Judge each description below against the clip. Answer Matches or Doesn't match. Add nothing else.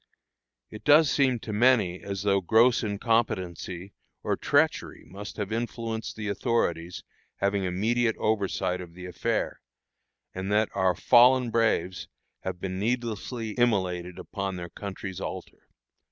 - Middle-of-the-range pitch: Doesn't match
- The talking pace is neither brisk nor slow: Doesn't match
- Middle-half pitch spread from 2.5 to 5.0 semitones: Matches